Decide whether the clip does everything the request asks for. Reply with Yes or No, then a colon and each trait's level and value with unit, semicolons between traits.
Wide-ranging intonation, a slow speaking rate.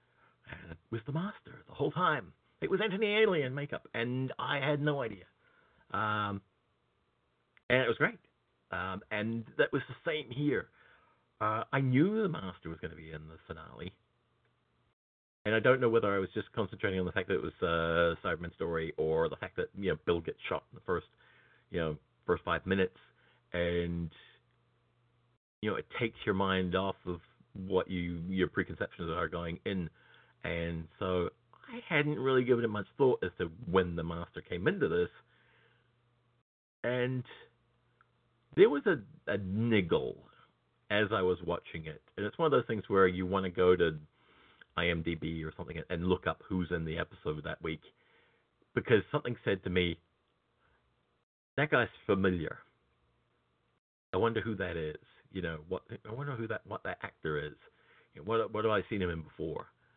No: wide, 5.7 semitones; average, 180 wpm